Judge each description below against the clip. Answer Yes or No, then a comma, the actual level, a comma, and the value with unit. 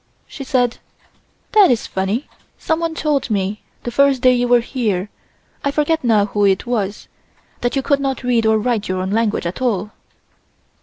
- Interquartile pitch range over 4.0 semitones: Yes, average, 4.7 semitones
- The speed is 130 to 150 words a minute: No, average, 175 wpm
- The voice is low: No, high, 240 Hz